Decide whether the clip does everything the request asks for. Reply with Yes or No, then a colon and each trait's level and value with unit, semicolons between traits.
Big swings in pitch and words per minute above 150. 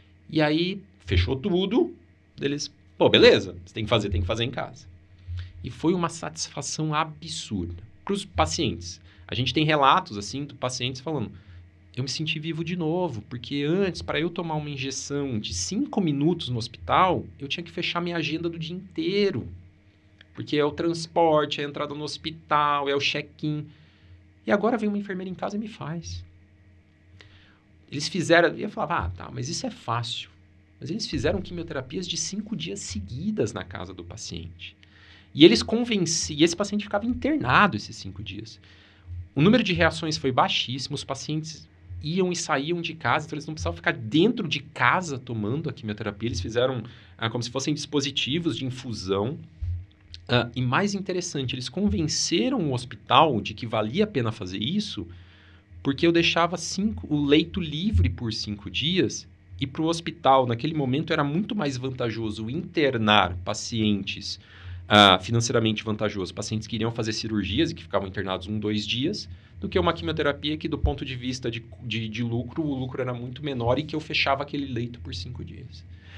Yes: wide, 7.9 semitones; average, 175 wpm